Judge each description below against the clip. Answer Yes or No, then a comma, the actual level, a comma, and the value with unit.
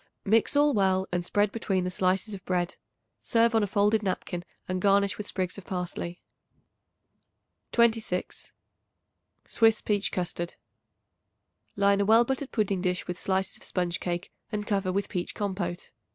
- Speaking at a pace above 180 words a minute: No, average, 150 wpm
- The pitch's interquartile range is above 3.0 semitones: No, narrow, 2.5 semitones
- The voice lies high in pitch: Yes, high, 195 Hz